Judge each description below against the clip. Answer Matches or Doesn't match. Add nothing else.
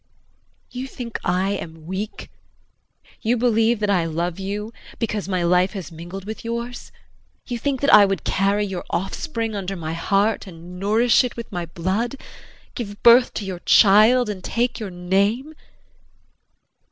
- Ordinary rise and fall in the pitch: Matches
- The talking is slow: Doesn't match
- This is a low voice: Doesn't match